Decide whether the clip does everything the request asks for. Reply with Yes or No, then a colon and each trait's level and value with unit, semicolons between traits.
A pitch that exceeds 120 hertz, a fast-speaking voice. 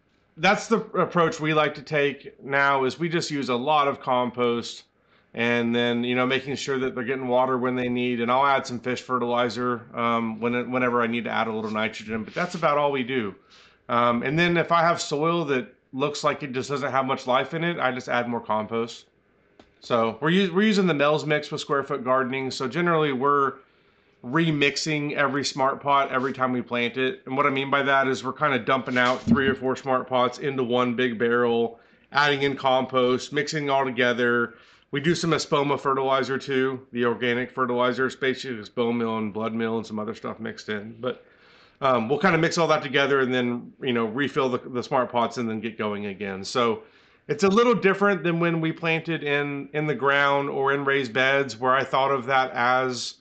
Yes: low, 130 Hz; fast, 220 wpm